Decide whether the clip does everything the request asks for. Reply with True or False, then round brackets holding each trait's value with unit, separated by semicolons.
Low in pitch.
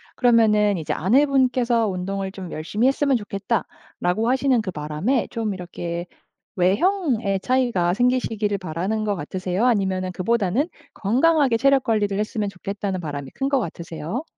False (210 Hz)